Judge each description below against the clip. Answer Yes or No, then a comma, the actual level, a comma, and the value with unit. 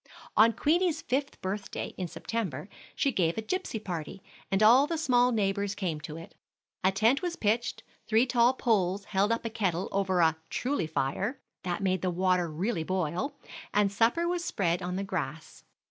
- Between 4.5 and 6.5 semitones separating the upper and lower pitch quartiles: Yes, average, 5.0 semitones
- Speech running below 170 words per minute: No, average, 175 wpm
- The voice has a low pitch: No, high, 200 Hz